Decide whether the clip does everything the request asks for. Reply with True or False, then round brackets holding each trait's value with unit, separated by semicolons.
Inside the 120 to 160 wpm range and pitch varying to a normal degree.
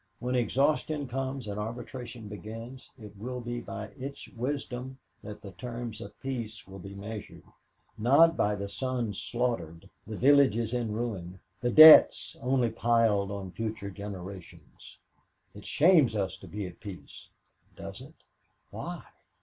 True (140 wpm; 3.8 semitones)